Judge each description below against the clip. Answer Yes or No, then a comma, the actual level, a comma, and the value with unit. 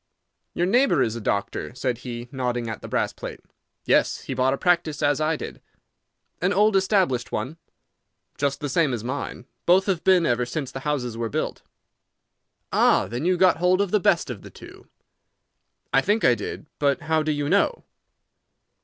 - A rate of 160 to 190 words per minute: Yes, average, 185 wpm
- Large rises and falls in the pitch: Yes, wide, 6.4 semitones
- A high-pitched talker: No, medium, 145 Hz